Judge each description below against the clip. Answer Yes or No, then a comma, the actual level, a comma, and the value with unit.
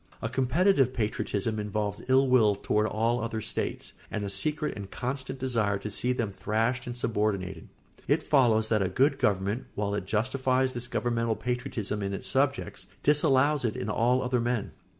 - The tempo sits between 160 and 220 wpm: Yes, average, 170 wpm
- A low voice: Yes, low, 115 Hz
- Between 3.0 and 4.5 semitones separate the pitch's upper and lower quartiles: Yes, average, 3.7 semitones